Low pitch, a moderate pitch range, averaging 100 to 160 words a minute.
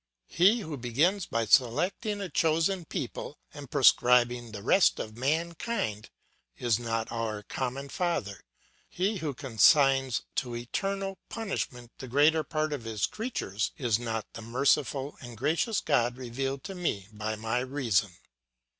No: low, 130 Hz; wide, 5.8 semitones; average, 140 wpm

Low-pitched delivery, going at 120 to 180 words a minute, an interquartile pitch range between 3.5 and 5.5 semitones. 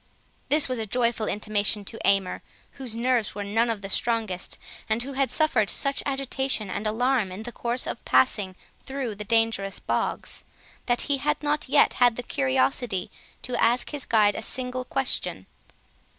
No: high, 230 Hz; average, 170 wpm; average, 3.9 semitones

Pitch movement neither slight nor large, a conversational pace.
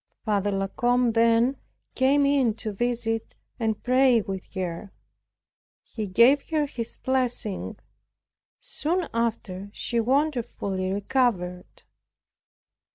No: average, 4.4 semitones; slow, 100 wpm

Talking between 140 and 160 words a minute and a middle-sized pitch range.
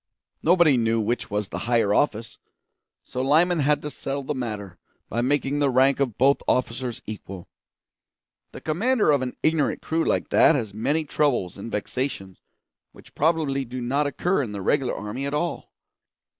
No: average, 170 wpm; average, 4.5 semitones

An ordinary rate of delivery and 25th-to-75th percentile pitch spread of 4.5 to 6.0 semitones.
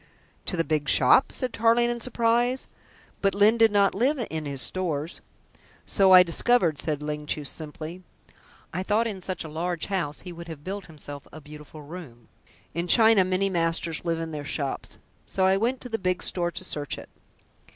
Yes: average, 190 wpm; average, 4.8 semitones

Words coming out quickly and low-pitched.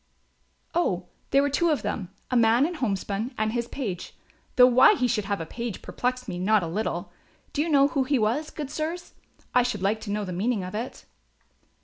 No: fast, 215 wpm; high, 240 Hz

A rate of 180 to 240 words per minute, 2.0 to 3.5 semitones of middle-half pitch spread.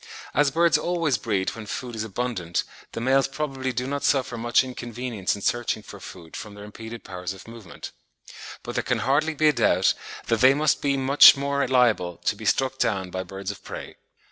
No: average, 200 wpm; average, 4.8 semitones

